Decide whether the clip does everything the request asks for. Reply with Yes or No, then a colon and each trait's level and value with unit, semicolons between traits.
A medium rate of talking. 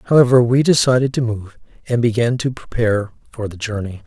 Yes: average, 175 wpm